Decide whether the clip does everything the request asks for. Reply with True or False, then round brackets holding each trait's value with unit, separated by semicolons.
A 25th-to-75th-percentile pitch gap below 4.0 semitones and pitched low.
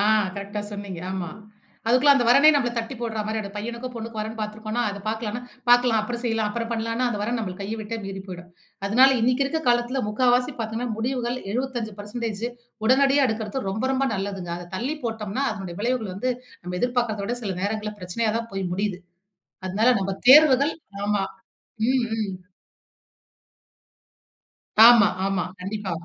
False (3.1 semitones; 225 Hz)